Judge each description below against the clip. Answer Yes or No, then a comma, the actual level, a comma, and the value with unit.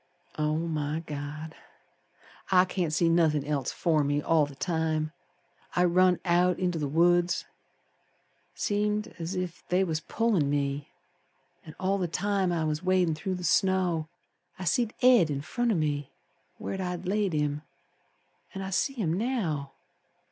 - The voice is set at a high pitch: No, medium, 170 Hz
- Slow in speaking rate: No, average, 155 wpm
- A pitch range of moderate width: Yes, average, 3.5 semitones